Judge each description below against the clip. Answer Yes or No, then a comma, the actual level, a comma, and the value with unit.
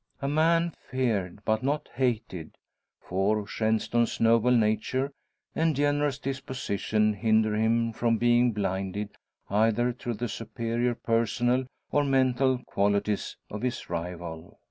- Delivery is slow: Yes, slow, 120 wpm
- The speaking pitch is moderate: No, low, 115 Hz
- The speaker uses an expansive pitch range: No, average, 3.4 semitones